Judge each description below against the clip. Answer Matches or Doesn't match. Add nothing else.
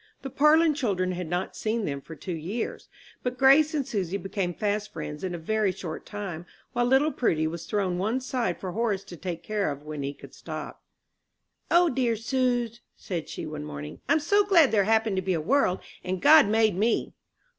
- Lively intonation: Matches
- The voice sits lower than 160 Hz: Doesn't match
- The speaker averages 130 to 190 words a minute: Doesn't match